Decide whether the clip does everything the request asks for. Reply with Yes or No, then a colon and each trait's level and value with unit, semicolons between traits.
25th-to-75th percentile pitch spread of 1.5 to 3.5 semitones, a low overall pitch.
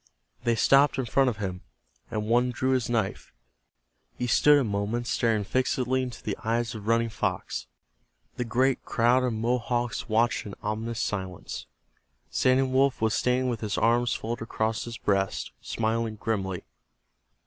Yes: narrow, 2.4 semitones; low, 115 Hz